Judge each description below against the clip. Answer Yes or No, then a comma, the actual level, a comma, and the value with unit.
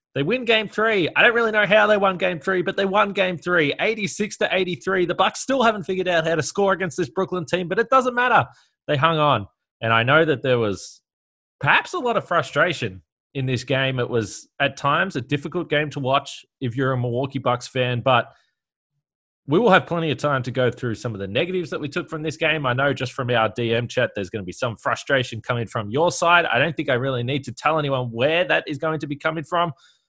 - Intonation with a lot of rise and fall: Yes, wide, 6.3 semitones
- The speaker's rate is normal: No, fast, 245 wpm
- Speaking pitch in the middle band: Yes, medium, 150 Hz